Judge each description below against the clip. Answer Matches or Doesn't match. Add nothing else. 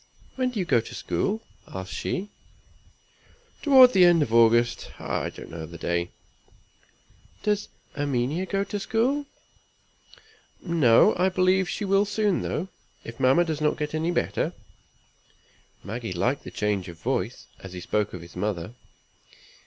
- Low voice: Doesn't match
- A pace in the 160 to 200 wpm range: Doesn't match